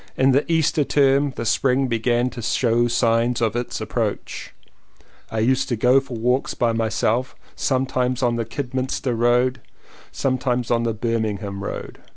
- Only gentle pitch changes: Yes, narrow, 2.2 semitones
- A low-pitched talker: Yes, low, 125 Hz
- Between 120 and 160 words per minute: Yes, average, 155 wpm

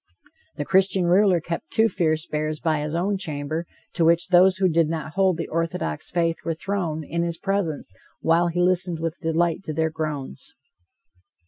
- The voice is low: No, medium, 165 Hz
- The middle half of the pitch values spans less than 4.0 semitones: Yes, narrow, 2.4 semitones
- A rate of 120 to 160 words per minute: No, average, 180 wpm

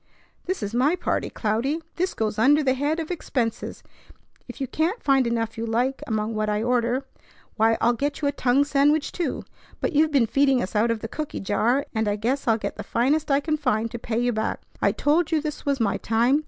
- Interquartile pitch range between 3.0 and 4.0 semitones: No, average, 4.4 semitones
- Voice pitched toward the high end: Yes, very high, 255 Hz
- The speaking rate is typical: No, fast, 225 wpm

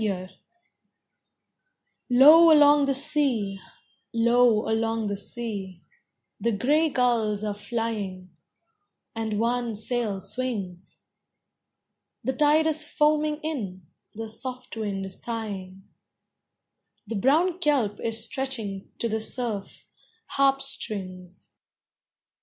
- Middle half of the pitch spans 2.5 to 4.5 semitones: No, average, 4.9 semitones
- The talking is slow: Yes, slow, 100 wpm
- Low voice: No, high, 230 Hz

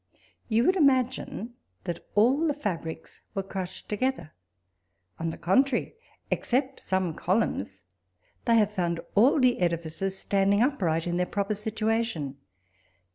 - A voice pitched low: No, high, 205 Hz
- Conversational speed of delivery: No, slow, 130 wpm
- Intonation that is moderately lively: No, wide, 6.1 semitones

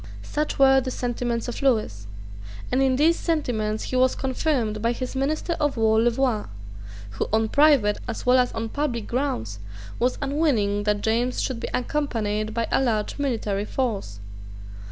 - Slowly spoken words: No, average, 160 wpm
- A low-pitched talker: No, high, 245 Hz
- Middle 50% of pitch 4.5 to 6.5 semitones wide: No, average, 3.8 semitones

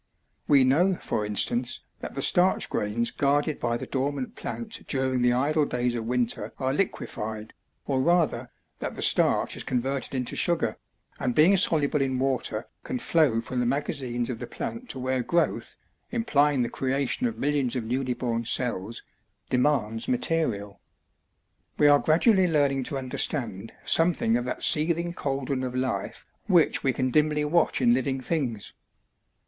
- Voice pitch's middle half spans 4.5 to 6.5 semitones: No, average, 4.0 semitones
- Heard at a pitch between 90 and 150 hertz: Yes, low, 135 Hz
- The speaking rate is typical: Yes, average, 160 wpm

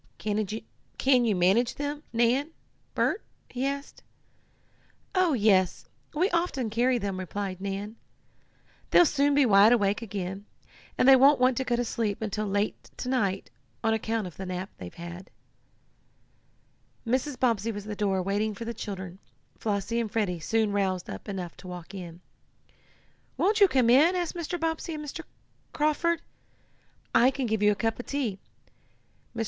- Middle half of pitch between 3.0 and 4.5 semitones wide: No, average, 5.1 semitones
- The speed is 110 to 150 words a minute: No, average, 165 wpm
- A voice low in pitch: No, high, 225 Hz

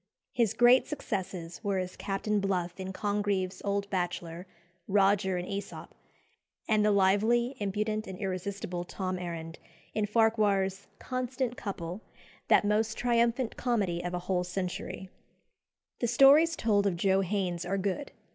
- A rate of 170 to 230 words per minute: No, slow, 135 wpm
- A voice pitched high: Yes, high, 200 Hz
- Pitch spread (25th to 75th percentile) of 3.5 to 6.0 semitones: No, average, 3.0 semitones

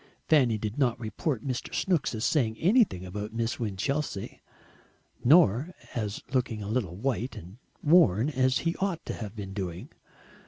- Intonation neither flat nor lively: No, wide, 5.7 semitones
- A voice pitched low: Yes, low, 120 Hz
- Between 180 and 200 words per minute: No, average, 155 wpm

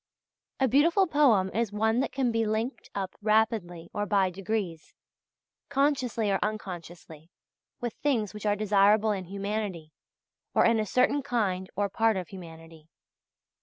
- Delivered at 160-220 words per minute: No, average, 145 wpm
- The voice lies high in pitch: Yes, high, 210 Hz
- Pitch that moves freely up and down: No, average, 3.5 semitones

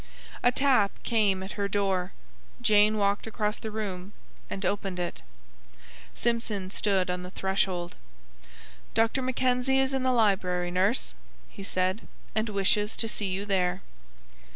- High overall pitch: Yes, high, 200 Hz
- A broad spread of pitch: No, average, 3.1 semitones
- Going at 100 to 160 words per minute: Yes, average, 140 wpm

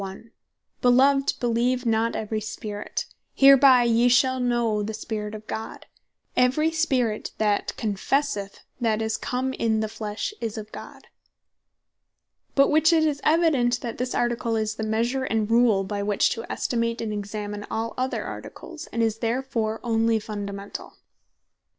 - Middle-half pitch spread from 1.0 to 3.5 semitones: Yes, average, 2.8 semitones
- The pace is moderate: Yes, average, 150 wpm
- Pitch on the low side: No, high, 230 Hz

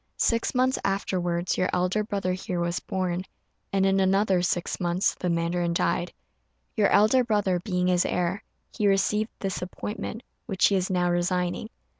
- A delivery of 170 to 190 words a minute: No, average, 160 wpm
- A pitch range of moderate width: No, narrow, 2.3 semitones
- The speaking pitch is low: No, medium, 185 Hz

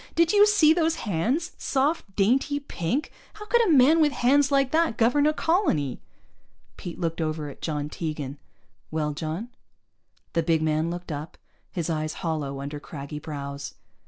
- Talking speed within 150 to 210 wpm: Yes, average, 160 wpm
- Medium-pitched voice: Yes, medium, 175 Hz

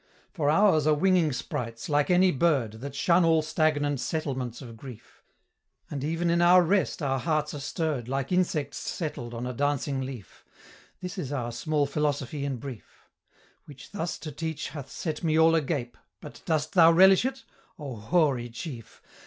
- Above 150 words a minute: Yes, average, 170 wpm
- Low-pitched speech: No, medium, 150 Hz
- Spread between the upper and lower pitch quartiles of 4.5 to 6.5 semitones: No, average, 3.8 semitones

